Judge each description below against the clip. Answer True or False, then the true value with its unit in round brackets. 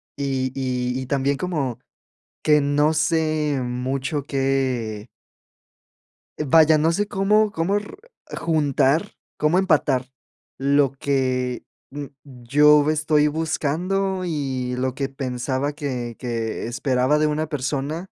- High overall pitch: False (140 Hz)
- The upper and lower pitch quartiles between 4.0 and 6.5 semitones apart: False (3.1 semitones)